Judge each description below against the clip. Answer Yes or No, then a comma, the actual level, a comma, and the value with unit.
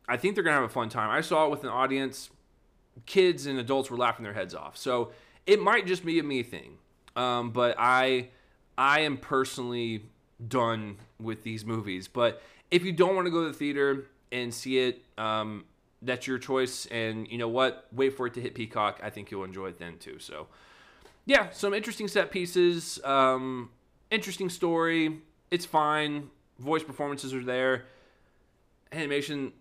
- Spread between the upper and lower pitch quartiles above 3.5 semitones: Yes, average, 4.6 semitones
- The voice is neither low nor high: No, low, 130 Hz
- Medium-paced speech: Yes, average, 180 wpm